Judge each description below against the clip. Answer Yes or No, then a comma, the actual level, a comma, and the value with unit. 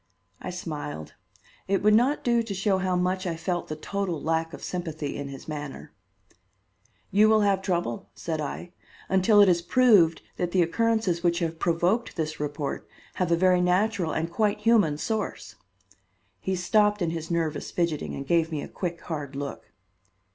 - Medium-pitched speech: Yes, medium, 175 Hz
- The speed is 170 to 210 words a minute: Yes, average, 175 wpm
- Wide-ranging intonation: No, average, 3.7 semitones